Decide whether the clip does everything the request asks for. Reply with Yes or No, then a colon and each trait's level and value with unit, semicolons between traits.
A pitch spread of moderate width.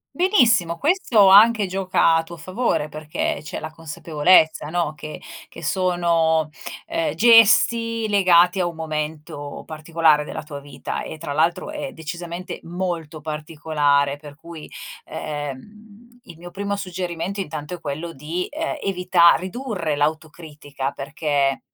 Yes: average, 4.1 semitones